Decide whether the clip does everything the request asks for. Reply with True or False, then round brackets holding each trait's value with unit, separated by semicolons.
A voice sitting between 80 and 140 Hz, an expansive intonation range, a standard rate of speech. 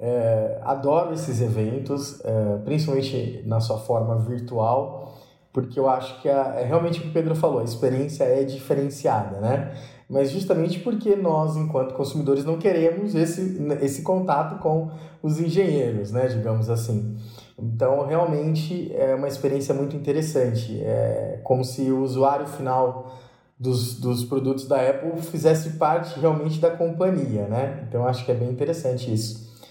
False (135 Hz; 4.3 semitones; 145 wpm)